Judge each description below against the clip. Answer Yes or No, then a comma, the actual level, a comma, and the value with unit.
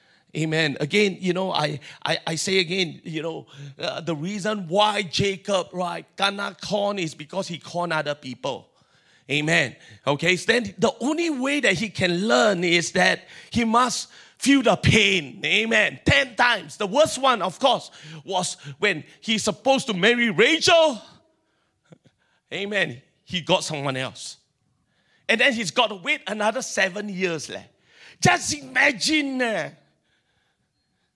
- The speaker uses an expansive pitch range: Yes, wide, 5.8 semitones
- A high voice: Yes, high, 195 Hz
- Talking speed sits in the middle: Yes, average, 145 wpm